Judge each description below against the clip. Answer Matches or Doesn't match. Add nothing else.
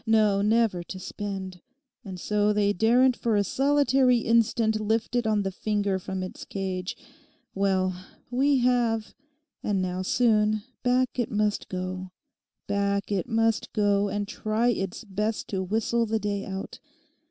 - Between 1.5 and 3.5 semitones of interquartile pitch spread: Matches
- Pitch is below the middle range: Doesn't match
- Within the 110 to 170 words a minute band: Matches